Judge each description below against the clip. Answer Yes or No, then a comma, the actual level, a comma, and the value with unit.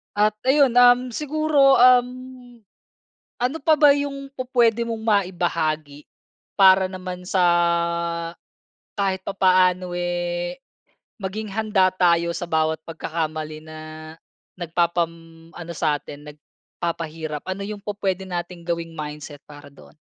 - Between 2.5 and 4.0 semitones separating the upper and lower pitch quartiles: No, wide, 5.5 semitones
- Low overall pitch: No, medium, 185 Hz